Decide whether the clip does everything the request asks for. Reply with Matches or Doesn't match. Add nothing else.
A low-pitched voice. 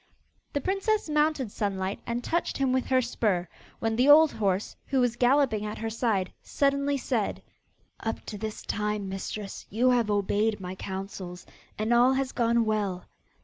Doesn't match